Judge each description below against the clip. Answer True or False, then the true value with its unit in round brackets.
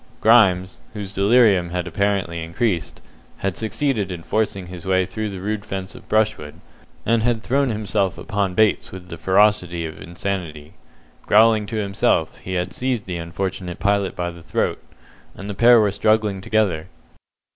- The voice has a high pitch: False (100 Hz)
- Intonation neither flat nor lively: True (3.3 semitones)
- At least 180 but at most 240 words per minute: False (160 wpm)